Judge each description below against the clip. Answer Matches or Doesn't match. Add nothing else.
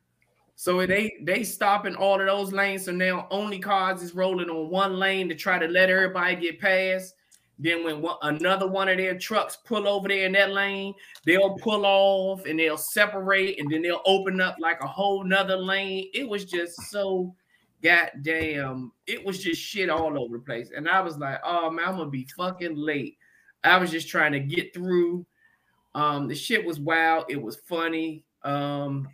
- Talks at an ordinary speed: Matches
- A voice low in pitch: Doesn't match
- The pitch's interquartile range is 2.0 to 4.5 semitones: Matches